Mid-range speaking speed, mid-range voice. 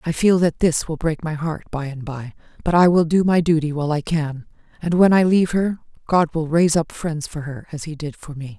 No: fast, 260 wpm; medium, 160 Hz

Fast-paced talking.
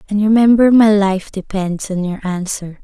No: average, 170 wpm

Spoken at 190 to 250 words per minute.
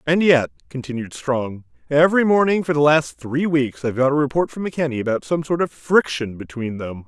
Yes: fast, 205 wpm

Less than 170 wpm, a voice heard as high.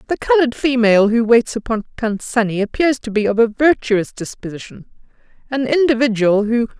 Yes: average, 160 wpm; high, 235 Hz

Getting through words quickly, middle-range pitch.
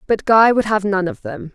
No: fast, 270 wpm; high, 195 Hz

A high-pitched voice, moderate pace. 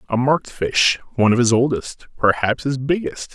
No: low, 130 Hz; average, 180 wpm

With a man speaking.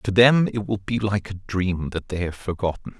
Yes: male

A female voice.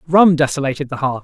No: male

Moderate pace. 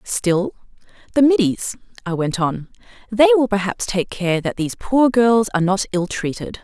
Yes: average, 165 wpm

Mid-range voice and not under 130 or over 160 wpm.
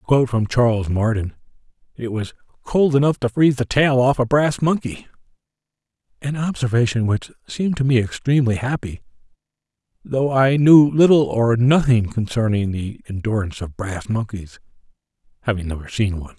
No: low, 120 Hz; average, 145 wpm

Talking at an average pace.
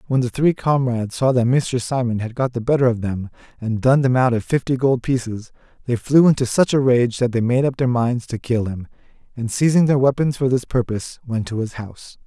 No: fast, 235 wpm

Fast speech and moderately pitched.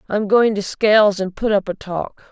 No: fast, 235 wpm; high, 205 Hz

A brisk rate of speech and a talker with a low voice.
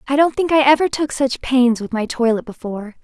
No: fast, 235 wpm; very high, 260 Hz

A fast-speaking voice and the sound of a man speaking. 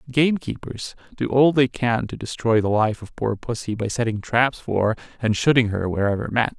No: average, 190 wpm; male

